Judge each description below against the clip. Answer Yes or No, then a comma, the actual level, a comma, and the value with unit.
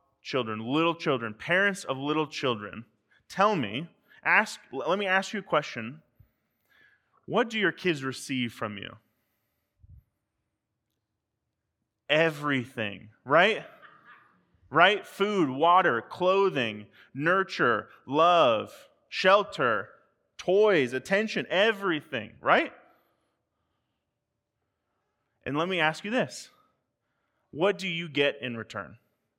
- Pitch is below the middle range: No, medium, 150 Hz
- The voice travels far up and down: Yes, wide, 8.2 semitones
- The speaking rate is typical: No, slow, 100 wpm